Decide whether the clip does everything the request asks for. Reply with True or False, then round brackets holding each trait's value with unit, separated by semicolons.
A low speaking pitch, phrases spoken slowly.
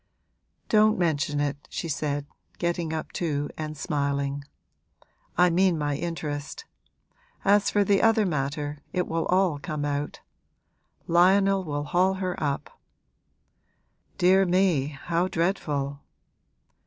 False (165 Hz; 115 wpm)